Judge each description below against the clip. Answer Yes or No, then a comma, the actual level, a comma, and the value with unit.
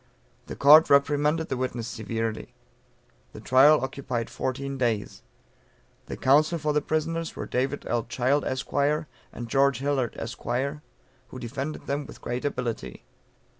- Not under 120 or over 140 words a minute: Yes, slow, 135 wpm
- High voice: No, low, 135 Hz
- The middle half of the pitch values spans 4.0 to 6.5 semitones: No, average, 3.3 semitones